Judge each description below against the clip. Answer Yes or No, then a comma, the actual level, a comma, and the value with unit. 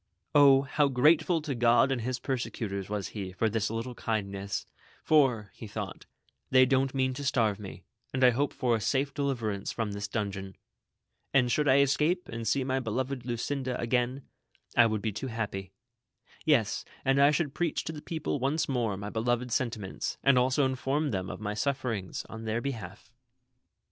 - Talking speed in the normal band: Yes, average, 180 wpm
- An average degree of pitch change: Yes, average, 4.0 semitones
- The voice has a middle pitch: No, low, 125 Hz